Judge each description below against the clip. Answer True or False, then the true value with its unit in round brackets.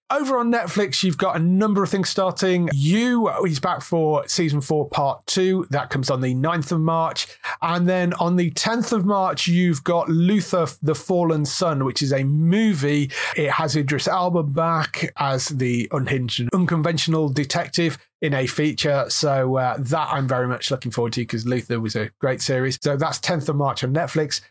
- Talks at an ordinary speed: True (190 wpm)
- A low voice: False (160 Hz)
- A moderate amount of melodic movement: True (4.5 semitones)